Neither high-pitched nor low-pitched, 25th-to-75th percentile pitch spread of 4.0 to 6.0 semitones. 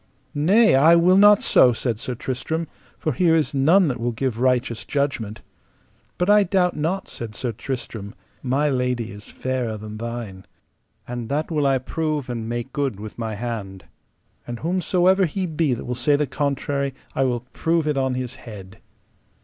No: low, 130 Hz; average, 5.0 semitones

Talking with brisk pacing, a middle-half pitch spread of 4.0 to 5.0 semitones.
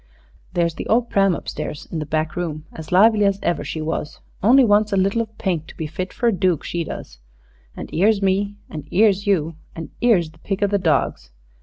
Yes: fast, 220 wpm; average, 4.3 semitones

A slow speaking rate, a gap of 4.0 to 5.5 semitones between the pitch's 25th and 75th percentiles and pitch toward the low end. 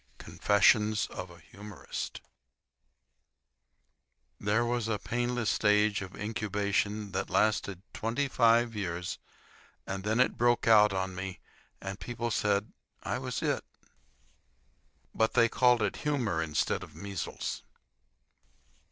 No: slow, 115 wpm; average, 2.9 semitones; low, 105 Hz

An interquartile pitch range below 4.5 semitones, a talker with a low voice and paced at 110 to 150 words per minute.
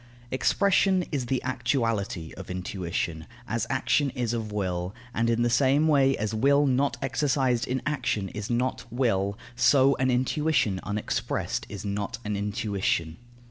No: average, 4.8 semitones; low, 120 Hz; average, 145 wpm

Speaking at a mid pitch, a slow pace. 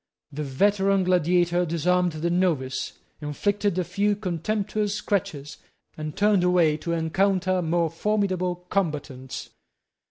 Yes: medium, 180 Hz; slow, 115 wpm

